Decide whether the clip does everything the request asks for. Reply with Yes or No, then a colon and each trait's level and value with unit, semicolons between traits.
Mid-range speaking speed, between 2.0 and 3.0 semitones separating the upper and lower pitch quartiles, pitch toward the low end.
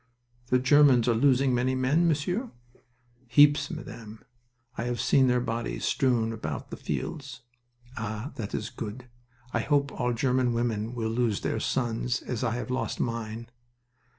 Yes: average, 150 wpm; narrow, 2.6 semitones; low, 125 Hz